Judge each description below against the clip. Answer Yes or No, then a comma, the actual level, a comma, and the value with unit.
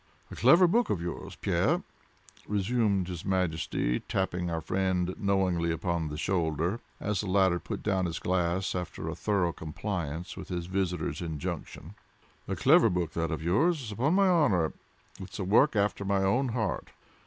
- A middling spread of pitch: Yes, average, 3.2 semitones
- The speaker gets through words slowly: No, average, 165 wpm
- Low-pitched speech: Yes, very low, 95 Hz